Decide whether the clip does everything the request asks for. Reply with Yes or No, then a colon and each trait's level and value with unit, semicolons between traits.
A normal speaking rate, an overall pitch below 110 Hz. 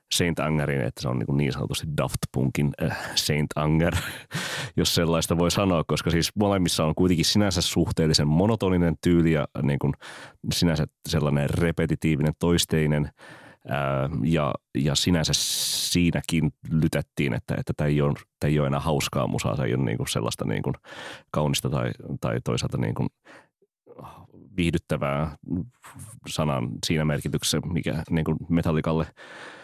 Yes: average, 140 wpm; very low, 80 Hz